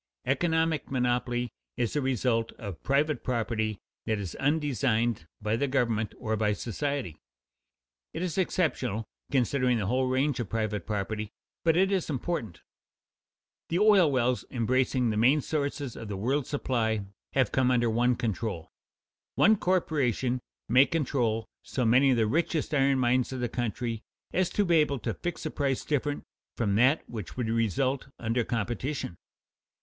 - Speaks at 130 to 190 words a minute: Yes, average, 155 wpm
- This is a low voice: Yes, low, 125 Hz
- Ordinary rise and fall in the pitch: Yes, average, 4.0 semitones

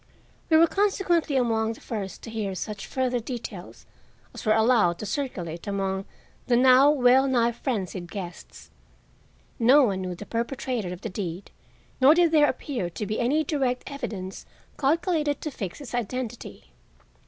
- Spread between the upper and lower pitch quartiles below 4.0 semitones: No, wide, 5.6 semitones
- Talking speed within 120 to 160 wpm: Yes, average, 155 wpm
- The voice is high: Yes, high, 235 Hz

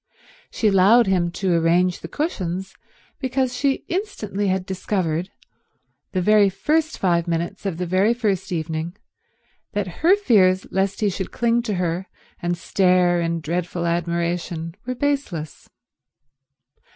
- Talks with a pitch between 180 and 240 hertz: Yes, medium, 185 Hz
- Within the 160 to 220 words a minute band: No, slow, 135 wpm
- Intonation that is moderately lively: Yes, average, 3.8 semitones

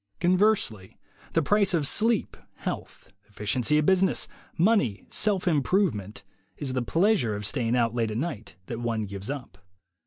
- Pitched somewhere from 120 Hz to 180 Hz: Yes, low, 135 Hz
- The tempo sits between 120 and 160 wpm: Yes, average, 150 wpm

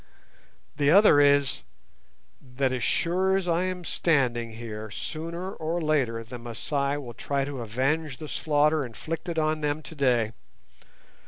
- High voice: No, medium, 145 Hz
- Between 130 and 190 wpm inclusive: Yes, average, 140 wpm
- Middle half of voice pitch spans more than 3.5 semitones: Yes, average, 4.4 semitones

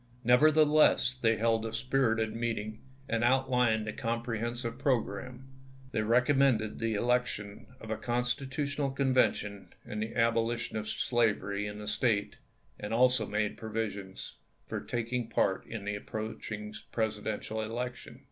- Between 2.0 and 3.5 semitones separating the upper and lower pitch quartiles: Yes, narrow, 2.5 semitones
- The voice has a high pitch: No, low, 115 Hz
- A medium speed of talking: No, slow, 130 wpm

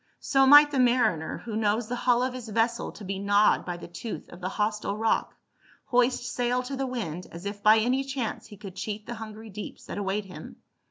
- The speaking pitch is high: Yes, high, 220 Hz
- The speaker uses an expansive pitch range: No, average, 3.4 semitones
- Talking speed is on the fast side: Yes, fast, 225 wpm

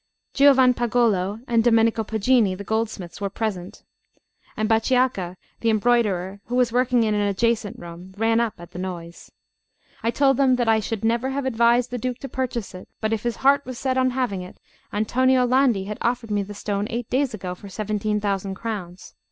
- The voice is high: Yes, high, 225 Hz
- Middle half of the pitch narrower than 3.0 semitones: No, average, 3.6 semitones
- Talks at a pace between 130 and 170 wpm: No, average, 185 wpm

